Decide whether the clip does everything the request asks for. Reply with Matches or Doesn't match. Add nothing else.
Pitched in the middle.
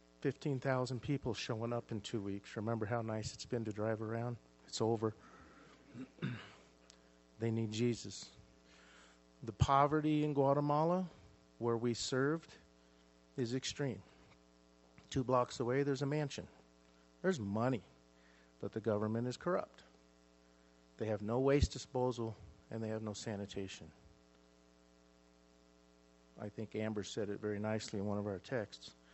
Doesn't match